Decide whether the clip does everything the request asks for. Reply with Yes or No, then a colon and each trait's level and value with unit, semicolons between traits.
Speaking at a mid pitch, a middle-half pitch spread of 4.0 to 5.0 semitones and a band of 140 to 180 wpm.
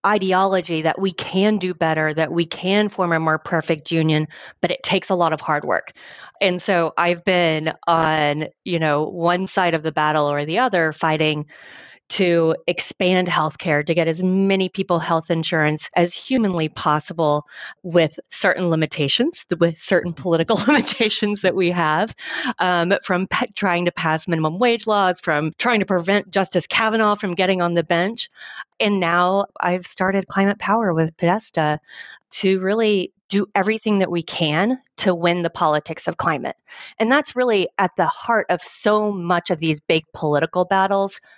No: medium, 180 Hz; average, 3.3 semitones; average, 170 wpm